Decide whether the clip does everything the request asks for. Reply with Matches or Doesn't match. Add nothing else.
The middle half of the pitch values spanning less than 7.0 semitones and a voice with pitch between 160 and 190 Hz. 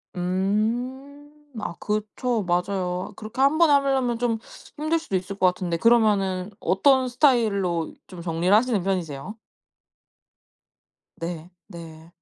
Doesn't match